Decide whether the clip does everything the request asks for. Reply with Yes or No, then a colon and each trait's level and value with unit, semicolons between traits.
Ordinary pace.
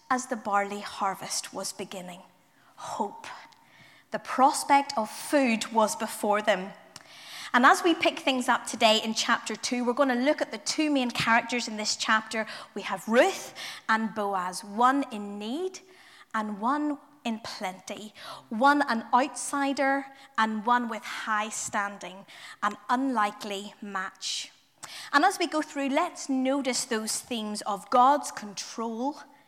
Yes: average, 145 wpm